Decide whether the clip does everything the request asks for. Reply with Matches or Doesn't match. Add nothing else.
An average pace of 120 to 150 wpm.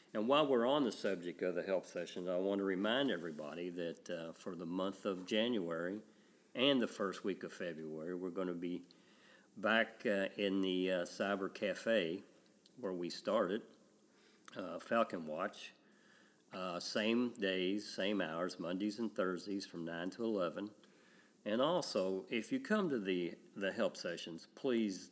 Doesn't match